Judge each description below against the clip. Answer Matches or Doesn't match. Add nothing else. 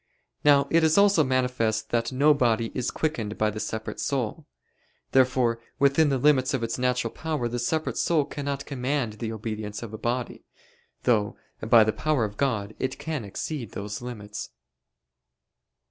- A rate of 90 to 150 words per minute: Doesn't match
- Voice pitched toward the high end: Doesn't match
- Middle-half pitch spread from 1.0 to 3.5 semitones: Doesn't match